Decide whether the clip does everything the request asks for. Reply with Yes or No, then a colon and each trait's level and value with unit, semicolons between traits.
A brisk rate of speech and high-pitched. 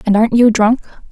Yes: fast, 215 wpm; high, 225 Hz